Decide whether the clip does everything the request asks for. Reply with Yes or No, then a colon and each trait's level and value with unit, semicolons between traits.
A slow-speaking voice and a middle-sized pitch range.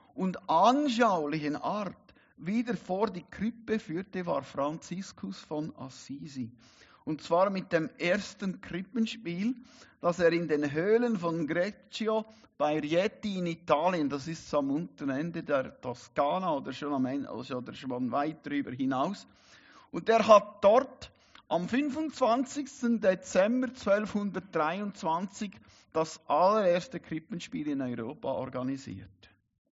No: slow, 120 wpm; wide, 6.6 semitones